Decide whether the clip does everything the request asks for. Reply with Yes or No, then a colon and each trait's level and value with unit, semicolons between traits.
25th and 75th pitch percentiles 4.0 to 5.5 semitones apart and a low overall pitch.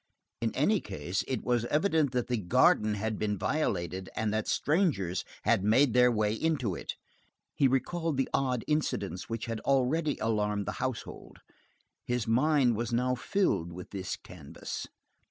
Yes: average, 4.8 semitones; low, 120 Hz